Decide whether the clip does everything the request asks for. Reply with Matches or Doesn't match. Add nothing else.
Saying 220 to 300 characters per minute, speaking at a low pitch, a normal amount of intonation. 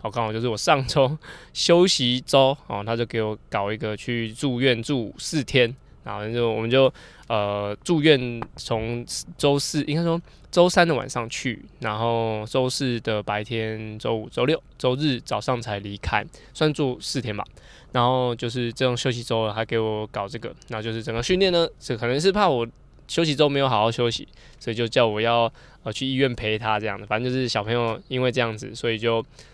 Matches